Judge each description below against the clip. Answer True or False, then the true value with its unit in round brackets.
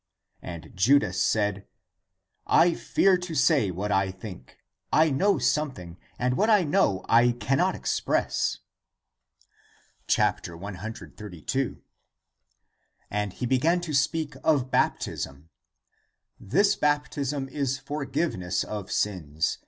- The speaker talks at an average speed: False (115 wpm)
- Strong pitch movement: True (7.7 semitones)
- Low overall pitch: True (125 Hz)